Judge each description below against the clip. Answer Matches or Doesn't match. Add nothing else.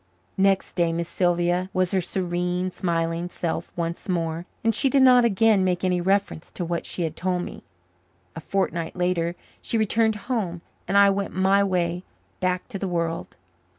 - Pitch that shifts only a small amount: Matches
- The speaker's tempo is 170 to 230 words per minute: Matches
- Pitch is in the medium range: Matches